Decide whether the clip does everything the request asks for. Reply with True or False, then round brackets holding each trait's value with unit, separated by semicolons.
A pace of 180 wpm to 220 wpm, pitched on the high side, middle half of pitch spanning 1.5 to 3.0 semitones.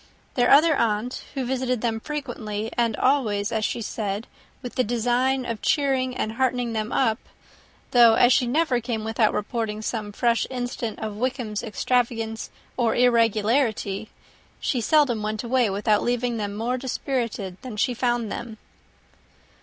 False (150 wpm; 235 Hz; 2.6 semitones)